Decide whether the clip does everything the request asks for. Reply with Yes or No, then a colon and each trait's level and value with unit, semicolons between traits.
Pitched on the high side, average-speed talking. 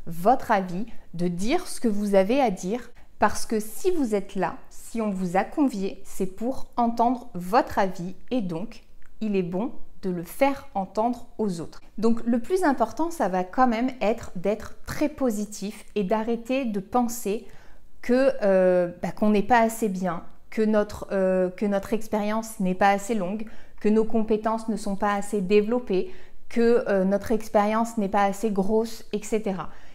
Yes: high, 215 Hz; average, 175 wpm